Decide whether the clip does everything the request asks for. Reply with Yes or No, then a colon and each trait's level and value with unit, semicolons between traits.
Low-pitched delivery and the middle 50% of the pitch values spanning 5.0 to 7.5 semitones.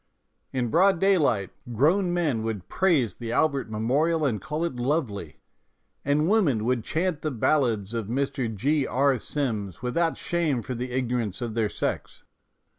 Yes: low, 130 Hz; wide, 5.5 semitones